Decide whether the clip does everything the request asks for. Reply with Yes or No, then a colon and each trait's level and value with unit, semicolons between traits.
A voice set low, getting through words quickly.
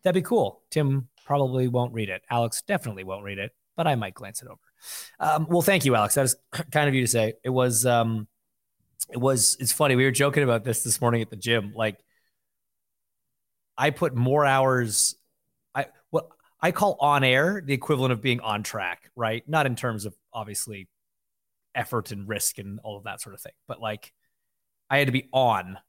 Yes: low, 125 Hz; fast, 210 wpm